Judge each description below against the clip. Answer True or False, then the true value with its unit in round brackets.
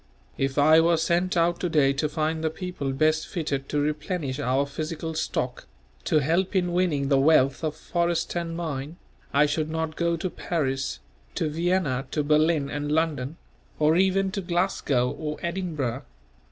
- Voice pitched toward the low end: False (155 Hz)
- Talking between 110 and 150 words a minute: False (165 wpm)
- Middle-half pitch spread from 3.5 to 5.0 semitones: False (3.1 semitones)